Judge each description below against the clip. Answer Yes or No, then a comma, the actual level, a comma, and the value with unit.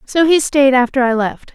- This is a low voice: No, very high, 265 Hz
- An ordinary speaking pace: No, fast, 235 wpm